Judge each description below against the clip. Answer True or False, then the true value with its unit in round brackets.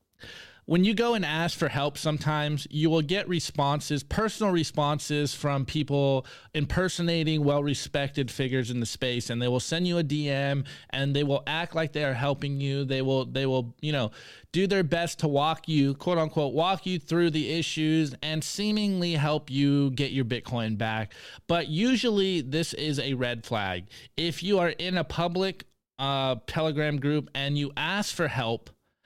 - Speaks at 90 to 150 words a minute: False (175 wpm)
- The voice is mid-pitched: True (150 Hz)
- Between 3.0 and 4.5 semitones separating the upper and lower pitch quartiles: True (3.5 semitones)